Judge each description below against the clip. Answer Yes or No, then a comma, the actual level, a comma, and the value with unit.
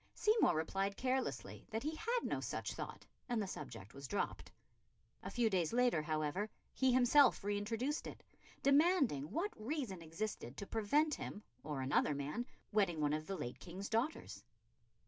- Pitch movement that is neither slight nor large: No, wide, 8.7 semitones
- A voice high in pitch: Yes, high, 210 Hz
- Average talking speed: Yes, average, 160 wpm